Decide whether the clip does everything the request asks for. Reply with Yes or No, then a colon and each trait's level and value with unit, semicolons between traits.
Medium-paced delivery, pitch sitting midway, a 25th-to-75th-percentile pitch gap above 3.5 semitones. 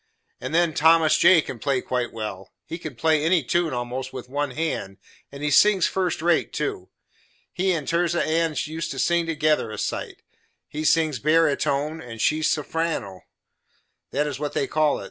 Yes: average, 180 wpm; medium, 155 Hz; average, 3.9 semitones